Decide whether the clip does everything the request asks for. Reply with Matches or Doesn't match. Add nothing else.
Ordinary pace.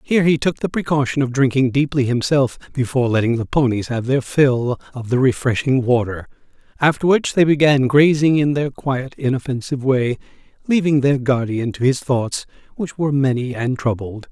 Matches